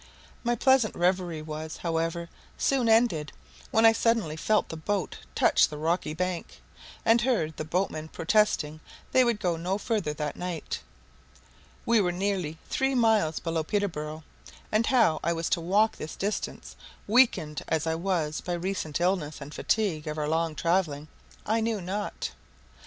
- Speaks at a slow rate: No, average, 155 wpm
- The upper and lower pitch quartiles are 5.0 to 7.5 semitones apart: Yes, average, 5.3 semitones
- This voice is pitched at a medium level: Yes, medium, 175 Hz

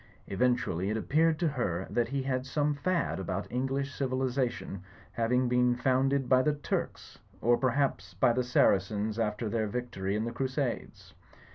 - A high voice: No, low, 125 Hz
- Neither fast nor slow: Yes, average, 160 wpm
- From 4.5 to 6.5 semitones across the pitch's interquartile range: No, average, 3.4 semitones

